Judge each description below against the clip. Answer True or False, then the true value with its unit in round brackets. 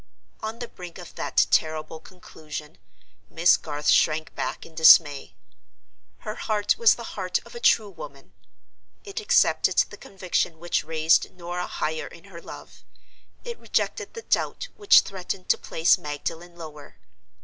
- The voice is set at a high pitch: False (170 Hz)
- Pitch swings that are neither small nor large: True (4.0 semitones)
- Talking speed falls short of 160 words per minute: True (150 wpm)